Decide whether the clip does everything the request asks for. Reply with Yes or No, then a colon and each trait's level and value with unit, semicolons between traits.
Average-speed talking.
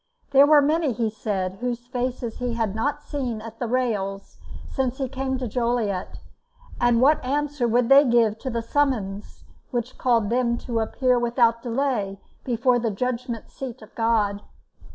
Yes: average, 165 wpm